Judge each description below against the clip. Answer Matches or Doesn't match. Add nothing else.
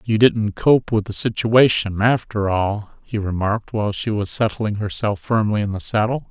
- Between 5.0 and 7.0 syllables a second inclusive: Doesn't match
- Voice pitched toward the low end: Matches